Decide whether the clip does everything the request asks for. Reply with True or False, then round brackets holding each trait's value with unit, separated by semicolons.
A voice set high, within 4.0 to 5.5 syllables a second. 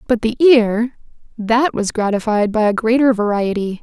True (225 Hz; 4.6 syllables/s)